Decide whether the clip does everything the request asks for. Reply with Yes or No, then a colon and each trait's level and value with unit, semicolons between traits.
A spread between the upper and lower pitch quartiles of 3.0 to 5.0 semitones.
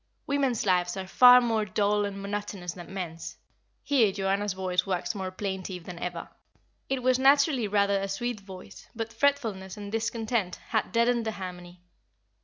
Yes: average, 3.7 semitones